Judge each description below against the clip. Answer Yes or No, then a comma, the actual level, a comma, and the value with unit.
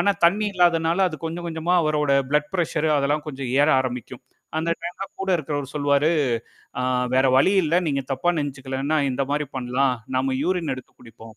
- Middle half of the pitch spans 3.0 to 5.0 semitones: Yes, average, 3.8 semitones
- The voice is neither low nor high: Yes, medium, 150 Hz